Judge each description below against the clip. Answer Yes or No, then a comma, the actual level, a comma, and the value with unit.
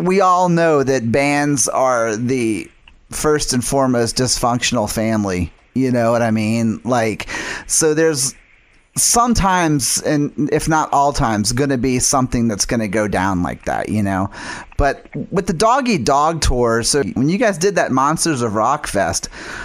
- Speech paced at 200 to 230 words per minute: No, average, 160 wpm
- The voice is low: Yes, low, 130 Hz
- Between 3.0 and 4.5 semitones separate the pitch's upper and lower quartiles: No, average, 5.1 semitones